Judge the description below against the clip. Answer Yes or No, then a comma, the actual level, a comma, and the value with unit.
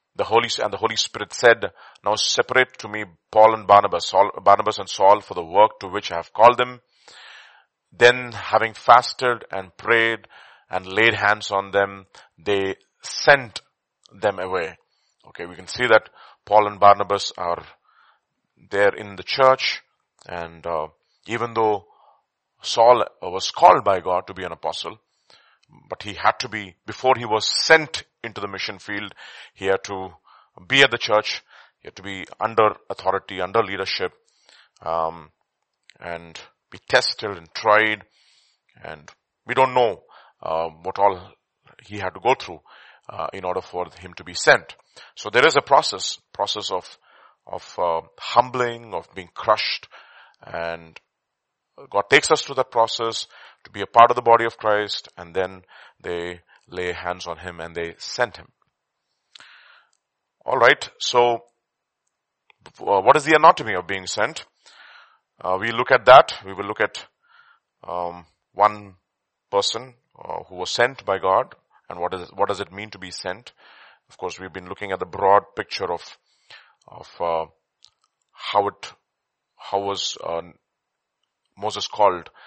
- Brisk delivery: No, average, 160 wpm